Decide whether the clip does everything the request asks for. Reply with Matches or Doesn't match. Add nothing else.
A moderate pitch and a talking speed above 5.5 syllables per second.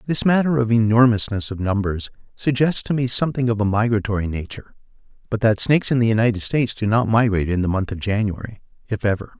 Doesn't match